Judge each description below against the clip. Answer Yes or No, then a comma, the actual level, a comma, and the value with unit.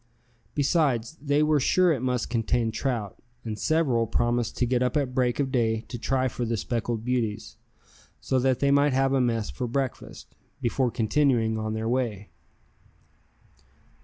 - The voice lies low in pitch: Yes, low, 125 Hz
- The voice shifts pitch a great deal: No, average, 2.9 semitones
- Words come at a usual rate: Yes, average, 160 wpm